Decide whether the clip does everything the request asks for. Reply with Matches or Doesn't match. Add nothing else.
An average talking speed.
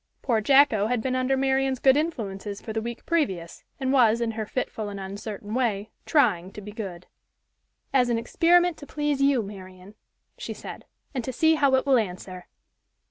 Matches